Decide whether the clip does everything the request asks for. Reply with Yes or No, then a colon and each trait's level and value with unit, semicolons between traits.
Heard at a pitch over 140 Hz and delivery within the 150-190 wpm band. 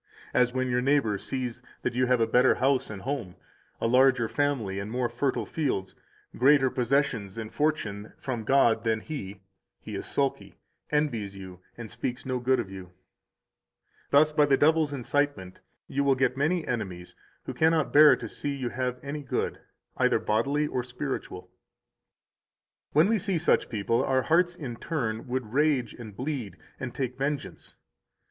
No: low, 130 Hz; average, 165 wpm